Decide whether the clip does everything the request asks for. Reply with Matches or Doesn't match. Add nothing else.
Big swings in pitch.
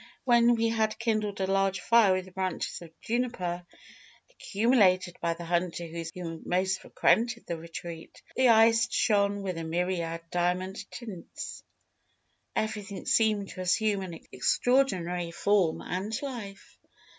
Doesn't match